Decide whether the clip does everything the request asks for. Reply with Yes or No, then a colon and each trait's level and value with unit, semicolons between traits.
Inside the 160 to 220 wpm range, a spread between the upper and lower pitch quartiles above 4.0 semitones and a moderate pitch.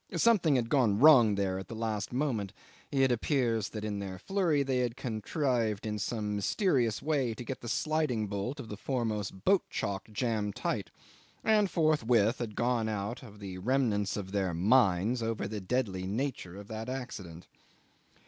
No: average, 170 wpm; average, 4.4 semitones; low, 115 Hz